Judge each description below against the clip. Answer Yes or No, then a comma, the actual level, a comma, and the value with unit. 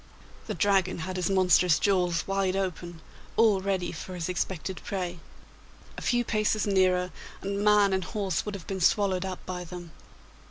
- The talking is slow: No, average, 165 wpm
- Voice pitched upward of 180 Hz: Yes, high, 190 Hz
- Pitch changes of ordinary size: No, narrow, 1.8 semitones